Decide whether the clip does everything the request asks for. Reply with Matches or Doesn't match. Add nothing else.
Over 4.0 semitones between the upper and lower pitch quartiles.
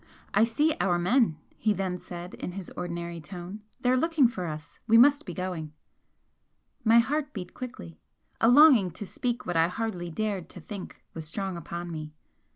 Matches